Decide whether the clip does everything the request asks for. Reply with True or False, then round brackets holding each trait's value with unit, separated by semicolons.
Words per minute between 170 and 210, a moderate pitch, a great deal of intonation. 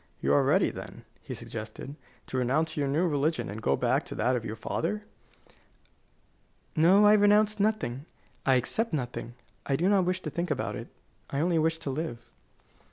True (180 wpm; 155 Hz; 6.2 semitones)